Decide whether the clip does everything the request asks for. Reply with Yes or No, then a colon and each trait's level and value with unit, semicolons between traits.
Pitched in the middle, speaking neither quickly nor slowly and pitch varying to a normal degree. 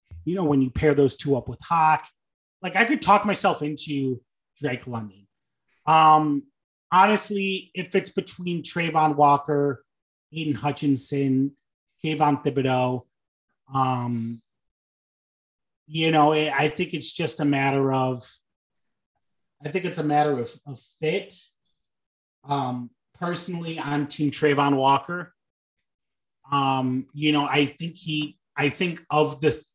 No: medium, 145 Hz; slow, 130 wpm; average, 3.3 semitones